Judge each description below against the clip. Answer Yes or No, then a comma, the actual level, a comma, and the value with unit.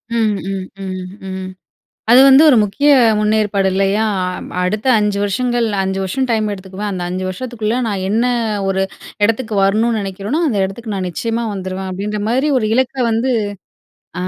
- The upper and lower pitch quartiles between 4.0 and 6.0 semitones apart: No, average, 3.3 semitones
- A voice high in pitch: Yes, high, 210 Hz